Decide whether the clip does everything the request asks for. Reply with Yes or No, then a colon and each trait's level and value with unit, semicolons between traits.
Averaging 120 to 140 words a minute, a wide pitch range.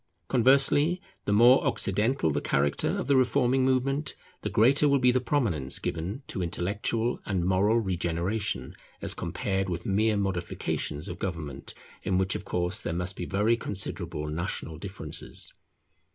No: average, 150 wpm; wide, 6.1 semitones